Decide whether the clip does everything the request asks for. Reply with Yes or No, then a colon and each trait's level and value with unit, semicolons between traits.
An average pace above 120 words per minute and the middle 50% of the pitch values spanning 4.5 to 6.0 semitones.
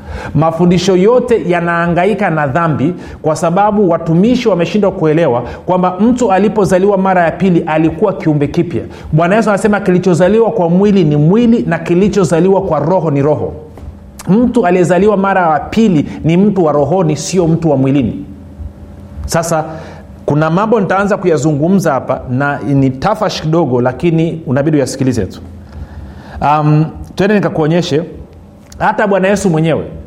Yes: average, 135 wpm; average, 5.1 semitones